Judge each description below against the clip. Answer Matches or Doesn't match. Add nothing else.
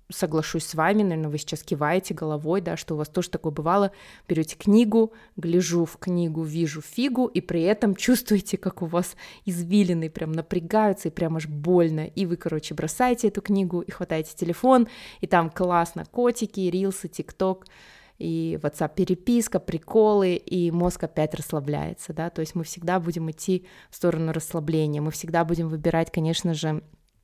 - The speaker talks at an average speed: Doesn't match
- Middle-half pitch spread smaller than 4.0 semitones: Matches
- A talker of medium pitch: Matches